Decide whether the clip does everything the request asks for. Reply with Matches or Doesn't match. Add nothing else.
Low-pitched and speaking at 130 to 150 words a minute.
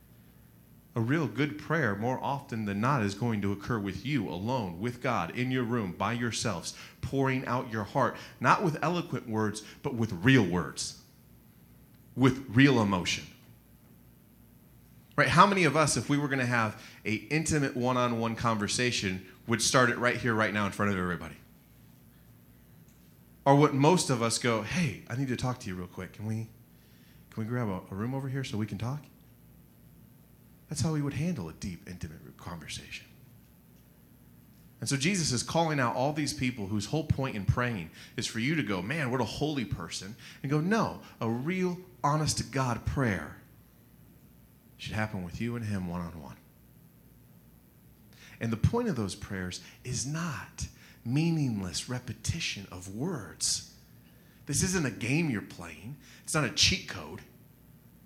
Doesn't match